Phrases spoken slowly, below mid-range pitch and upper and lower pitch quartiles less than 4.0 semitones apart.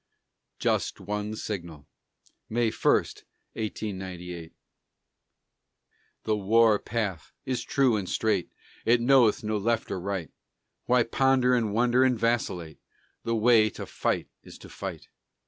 Yes: slow, 125 wpm; low, 110 Hz; average, 3.4 semitones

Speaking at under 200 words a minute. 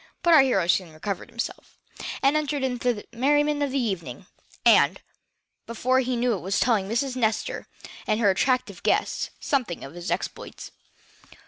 Yes: average, 165 wpm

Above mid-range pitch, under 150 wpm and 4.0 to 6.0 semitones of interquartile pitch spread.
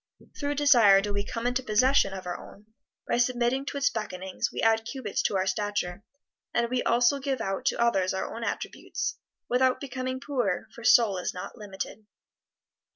No: high, 230 Hz; average, 180 wpm; average, 4.3 semitones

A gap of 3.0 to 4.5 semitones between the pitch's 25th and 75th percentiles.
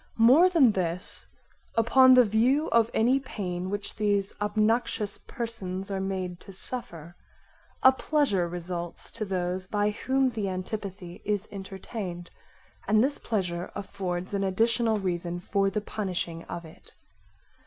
Yes: average, 3.9 semitones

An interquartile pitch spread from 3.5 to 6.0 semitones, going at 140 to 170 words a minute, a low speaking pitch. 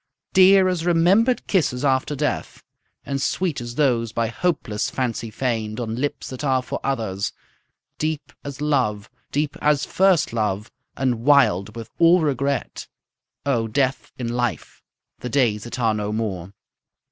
Yes: average, 4.7 semitones; average, 145 wpm; low, 130 Hz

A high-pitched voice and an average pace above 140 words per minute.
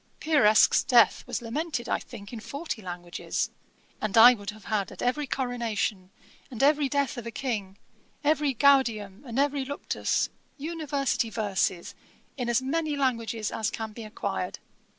Yes: high, 240 Hz; average, 150 wpm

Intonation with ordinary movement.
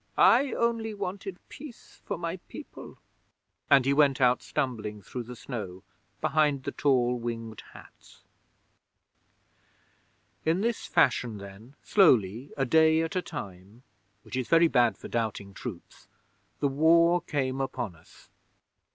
No: wide, 6.1 semitones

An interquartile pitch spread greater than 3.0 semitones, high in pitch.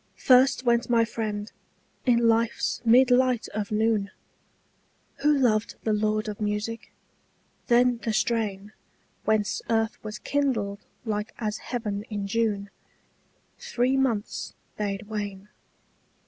No: narrow, 2.4 semitones; high, 220 Hz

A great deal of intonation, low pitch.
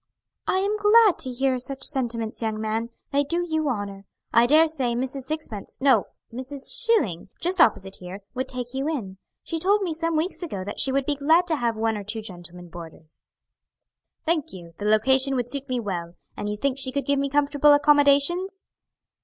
No: wide, 6.1 semitones; very high, 265 Hz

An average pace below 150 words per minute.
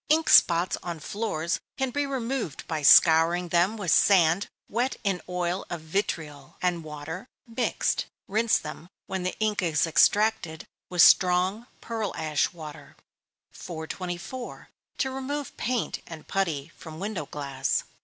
Yes: average, 140 wpm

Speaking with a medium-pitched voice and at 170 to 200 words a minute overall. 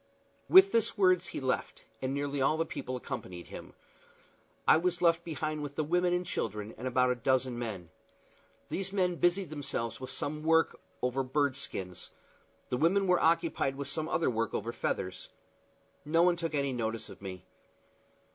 Yes: medium, 145 Hz; average, 175 wpm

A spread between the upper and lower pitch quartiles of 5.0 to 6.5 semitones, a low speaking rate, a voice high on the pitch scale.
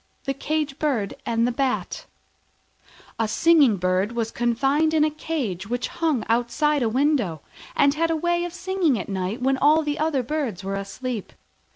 No: wide, 5.4 semitones; average, 170 wpm; very high, 265 Hz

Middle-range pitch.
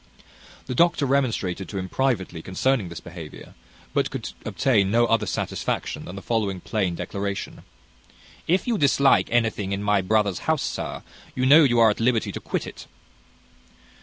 No: low, 110 Hz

